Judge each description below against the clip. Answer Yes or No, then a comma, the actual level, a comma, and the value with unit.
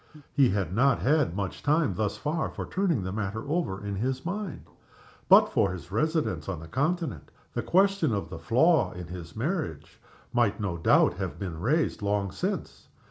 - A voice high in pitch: No, low, 110 Hz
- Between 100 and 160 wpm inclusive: No, average, 180 wpm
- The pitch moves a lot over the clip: Yes, wide, 8.7 semitones